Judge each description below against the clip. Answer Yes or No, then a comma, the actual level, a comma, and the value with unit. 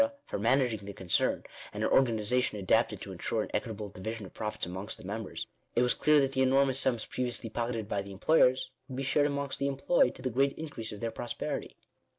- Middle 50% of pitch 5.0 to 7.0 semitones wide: No, average, 4.0 semitones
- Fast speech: Yes, fast, 215 wpm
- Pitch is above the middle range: No, low, 120 Hz